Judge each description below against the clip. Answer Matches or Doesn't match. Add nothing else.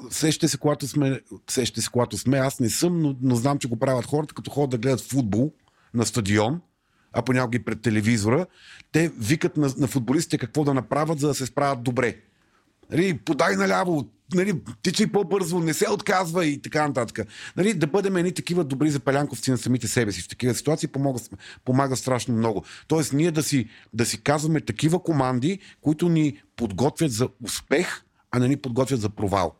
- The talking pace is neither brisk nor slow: Doesn't match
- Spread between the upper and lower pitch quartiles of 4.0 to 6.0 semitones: Matches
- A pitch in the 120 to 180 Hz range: Matches